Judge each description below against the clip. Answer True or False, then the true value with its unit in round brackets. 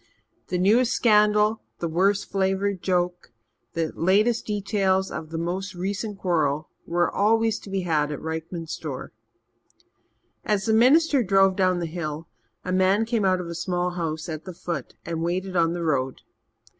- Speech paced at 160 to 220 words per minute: True (165 wpm)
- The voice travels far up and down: False (3.4 semitones)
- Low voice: False (185 Hz)